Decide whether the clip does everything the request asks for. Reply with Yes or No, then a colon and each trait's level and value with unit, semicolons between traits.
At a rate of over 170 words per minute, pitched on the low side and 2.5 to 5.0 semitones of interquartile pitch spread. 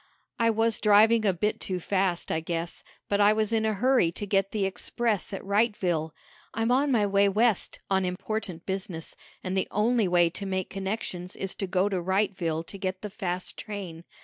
No: average, 195 wpm; high, 195 Hz; average, 2.8 semitones